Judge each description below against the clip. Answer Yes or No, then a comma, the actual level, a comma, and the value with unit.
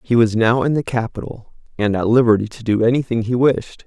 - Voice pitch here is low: Yes, low, 115 Hz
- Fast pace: Yes, fast, 215 wpm